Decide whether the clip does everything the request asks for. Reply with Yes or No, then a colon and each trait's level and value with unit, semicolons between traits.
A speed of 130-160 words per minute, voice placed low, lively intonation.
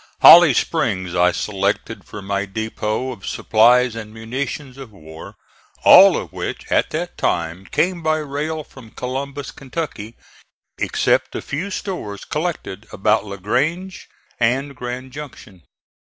Yes: slow, 135 wpm; low, 120 Hz; wide, 5.8 semitones